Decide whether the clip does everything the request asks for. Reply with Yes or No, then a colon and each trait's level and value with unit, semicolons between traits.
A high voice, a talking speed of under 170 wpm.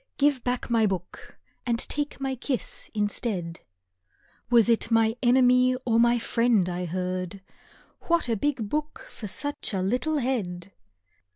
Yes: high, 235 Hz; average, 145 wpm